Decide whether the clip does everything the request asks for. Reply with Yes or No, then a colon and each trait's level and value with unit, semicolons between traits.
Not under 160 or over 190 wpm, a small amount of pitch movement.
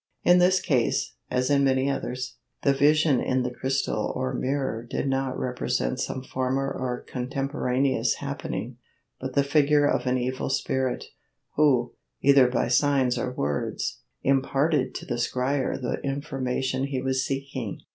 No: average, 145 wpm; narrow, 1.7 semitones